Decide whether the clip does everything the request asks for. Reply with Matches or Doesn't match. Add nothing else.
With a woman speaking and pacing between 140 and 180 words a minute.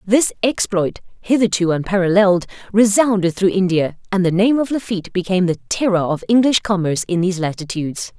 Matches